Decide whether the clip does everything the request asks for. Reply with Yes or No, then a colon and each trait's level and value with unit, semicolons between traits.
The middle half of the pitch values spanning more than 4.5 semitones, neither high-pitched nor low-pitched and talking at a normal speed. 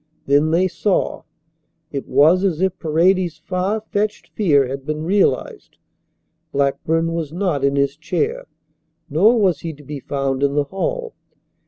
Yes: average, 5.2 semitones; medium, 165 Hz; average, 150 wpm